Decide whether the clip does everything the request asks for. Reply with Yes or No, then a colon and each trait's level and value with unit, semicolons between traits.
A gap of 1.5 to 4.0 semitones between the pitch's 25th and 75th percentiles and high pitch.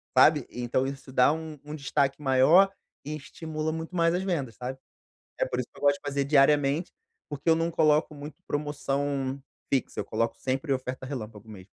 No: average, 2.8 semitones; medium, 140 Hz